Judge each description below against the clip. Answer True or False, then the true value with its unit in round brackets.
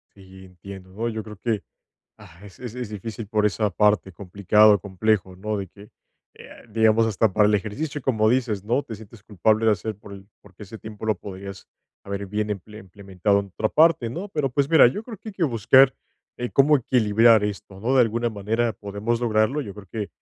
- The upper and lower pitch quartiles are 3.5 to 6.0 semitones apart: False (2.8 semitones)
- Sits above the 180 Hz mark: False (105 Hz)